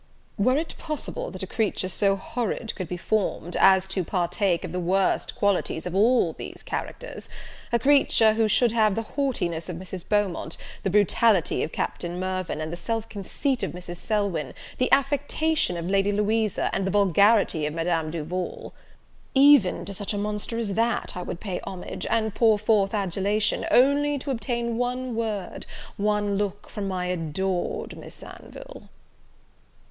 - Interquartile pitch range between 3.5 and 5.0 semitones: Yes, average, 4.0 semitones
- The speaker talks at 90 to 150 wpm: No, average, 165 wpm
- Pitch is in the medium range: No, high, 205 Hz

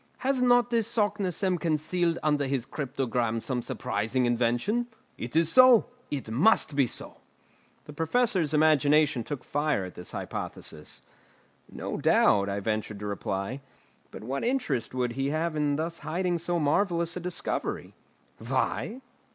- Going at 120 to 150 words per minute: Yes, average, 145 wpm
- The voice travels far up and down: Yes, wide, 6.6 semitones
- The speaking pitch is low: No, medium, 150 Hz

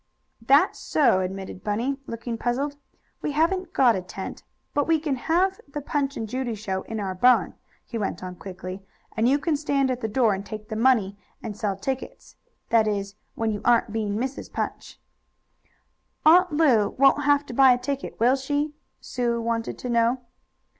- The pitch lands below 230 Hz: No, high, 240 Hz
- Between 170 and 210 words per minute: Yes, average, 180 wpm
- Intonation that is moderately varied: Yes, average, 4.8 semitones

